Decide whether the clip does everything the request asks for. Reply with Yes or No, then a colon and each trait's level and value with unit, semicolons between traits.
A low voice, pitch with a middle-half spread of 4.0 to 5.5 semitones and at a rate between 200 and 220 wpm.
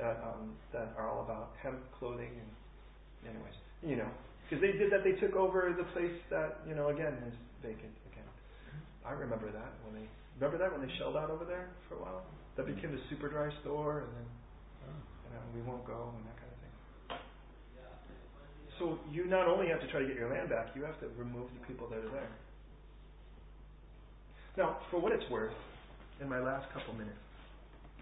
Yes: low, 130 Hz; average, 5.1 semitones; fast, 205 wpm